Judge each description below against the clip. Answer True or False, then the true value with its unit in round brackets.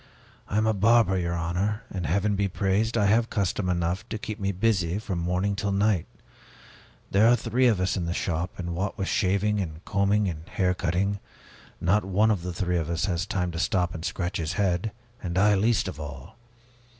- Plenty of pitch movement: False (3.0 semitones)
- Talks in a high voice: False (95 Hz)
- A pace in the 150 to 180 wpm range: False (205 wpm)